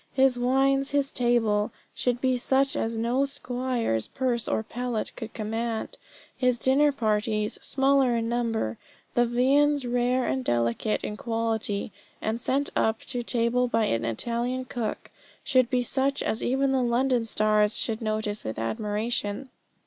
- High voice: Yes, high, 240 Hz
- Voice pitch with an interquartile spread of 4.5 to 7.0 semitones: No, average, 3.0 semitones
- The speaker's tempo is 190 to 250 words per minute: No, average, 150 wpm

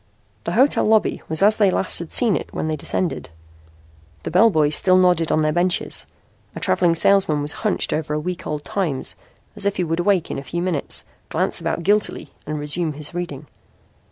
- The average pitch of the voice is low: No, medium, 175 Hz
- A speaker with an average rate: Yes, average, 195 wpm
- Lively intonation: No, average, 3.8 semitones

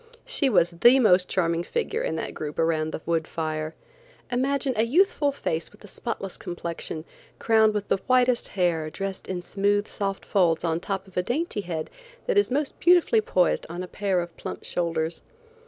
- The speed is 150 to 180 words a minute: No, average, 190 wpm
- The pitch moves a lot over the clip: Yes, wide, 6.7 semitones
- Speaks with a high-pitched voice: Yes, high, 195 Hz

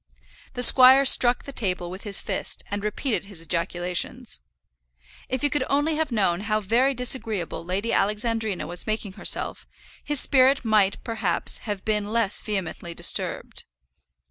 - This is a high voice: Yes, high, 215 Hz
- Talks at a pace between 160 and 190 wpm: No, average, 145 wpm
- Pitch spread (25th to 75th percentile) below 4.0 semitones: No, average, 4.7 semitones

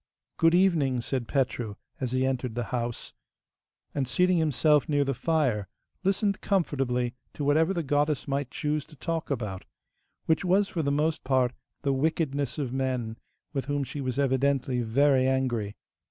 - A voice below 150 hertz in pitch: Yes, medium, 140 Hz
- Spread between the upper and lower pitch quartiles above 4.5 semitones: No, average, 3.4 semitones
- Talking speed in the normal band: Yes, average, 160 wpm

